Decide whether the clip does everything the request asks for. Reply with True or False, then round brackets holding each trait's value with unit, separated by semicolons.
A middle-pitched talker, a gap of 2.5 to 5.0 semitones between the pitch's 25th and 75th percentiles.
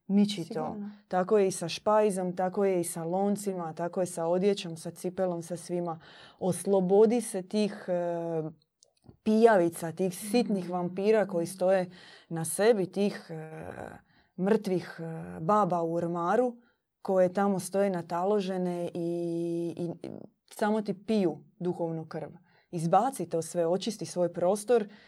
True (180 Hz; 3.0 semitones)